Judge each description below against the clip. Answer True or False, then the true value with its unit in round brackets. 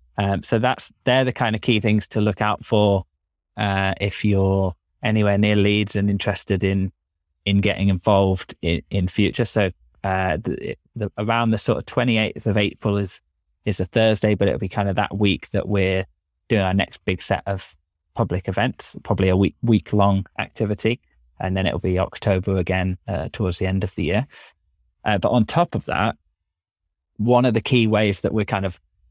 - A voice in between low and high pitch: False (100 Hz)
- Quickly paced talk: False (195 wpm)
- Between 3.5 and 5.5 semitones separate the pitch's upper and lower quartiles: False (2.5 semitones)